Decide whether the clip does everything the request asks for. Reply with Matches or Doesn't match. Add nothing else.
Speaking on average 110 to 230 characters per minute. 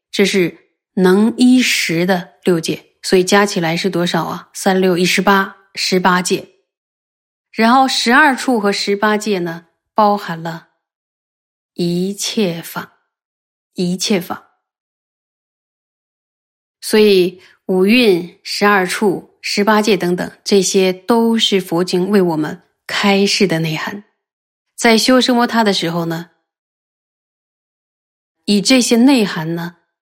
Matches